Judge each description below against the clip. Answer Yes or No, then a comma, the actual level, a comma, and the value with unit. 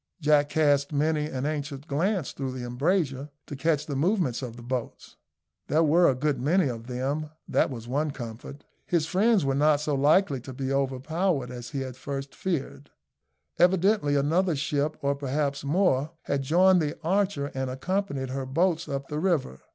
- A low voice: No, medium, 145 Hz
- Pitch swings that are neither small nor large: Yes, average, 3.3 semitones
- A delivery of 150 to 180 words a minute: Yes, average, 175 wpm